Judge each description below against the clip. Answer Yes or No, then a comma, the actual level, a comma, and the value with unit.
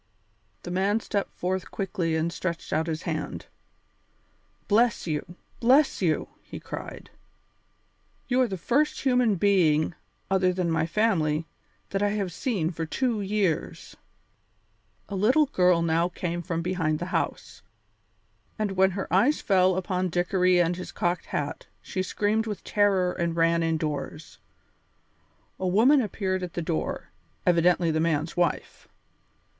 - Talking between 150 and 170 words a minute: No, average, 140 wpm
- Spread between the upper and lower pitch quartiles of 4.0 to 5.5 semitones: No, average, 3.4 semitones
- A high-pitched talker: No, medium, 180 Hz